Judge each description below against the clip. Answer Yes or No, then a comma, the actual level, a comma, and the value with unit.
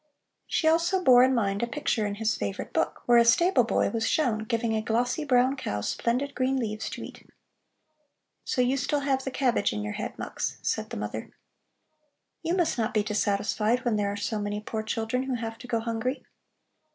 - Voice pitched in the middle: No, high, 235 Hz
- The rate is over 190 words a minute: Yes, average, 200 wpm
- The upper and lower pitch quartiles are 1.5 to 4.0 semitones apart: Yes, average, 3.5 semitones